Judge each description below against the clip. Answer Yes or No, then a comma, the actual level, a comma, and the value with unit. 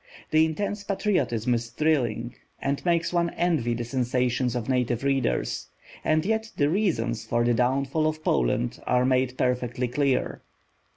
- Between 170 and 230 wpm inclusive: No, average, 150 wpm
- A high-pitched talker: No, low, 130 Hz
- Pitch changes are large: No, average, 4.6 semitones